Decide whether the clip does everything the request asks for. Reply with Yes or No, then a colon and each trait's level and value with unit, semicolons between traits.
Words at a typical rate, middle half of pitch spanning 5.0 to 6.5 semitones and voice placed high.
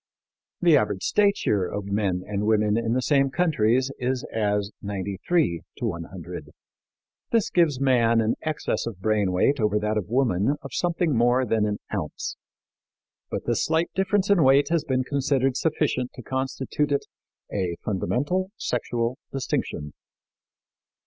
No: average, 145 wpm; wide, 5.4 semitones; low, 120 Hz